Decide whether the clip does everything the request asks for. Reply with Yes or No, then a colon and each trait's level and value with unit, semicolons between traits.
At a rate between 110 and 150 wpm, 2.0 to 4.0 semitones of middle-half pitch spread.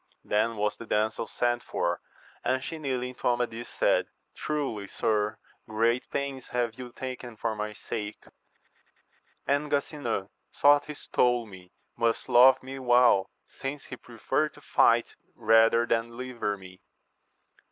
Yes: average, 140 wpm; average, 3.1 semitones